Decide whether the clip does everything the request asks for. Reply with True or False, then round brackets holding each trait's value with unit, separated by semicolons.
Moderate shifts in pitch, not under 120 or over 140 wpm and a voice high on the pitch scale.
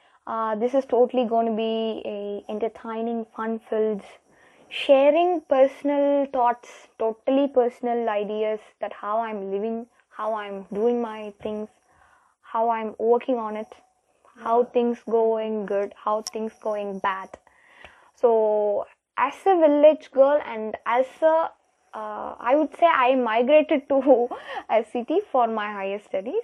True (3.8 semitones; 135 wpm; 230 Hz)